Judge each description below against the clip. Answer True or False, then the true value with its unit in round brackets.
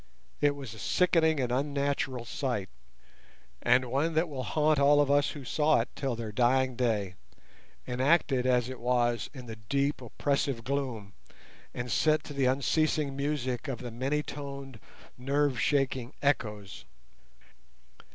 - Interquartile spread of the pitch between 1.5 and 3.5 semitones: True (2.9 semitones)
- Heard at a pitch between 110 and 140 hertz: True (135 Hz)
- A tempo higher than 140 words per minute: False (135 wpm)